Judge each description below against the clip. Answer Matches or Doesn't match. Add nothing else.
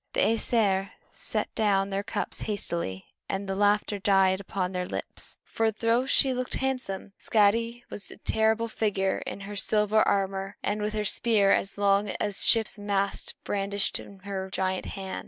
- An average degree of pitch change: Doesn't match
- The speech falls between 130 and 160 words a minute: Doesn't match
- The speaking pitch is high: Matches